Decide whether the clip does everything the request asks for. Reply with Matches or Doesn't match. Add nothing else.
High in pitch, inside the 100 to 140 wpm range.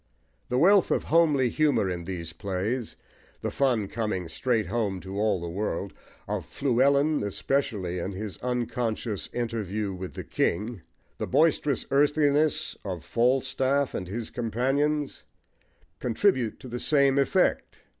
Doesn't match